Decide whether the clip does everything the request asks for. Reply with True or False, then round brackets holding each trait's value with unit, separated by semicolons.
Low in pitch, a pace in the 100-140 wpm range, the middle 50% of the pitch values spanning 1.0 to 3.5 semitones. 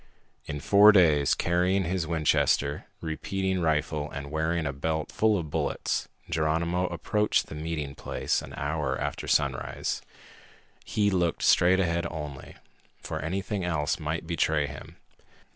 True (80 Hz; 135 wpm; 3.1 semitones)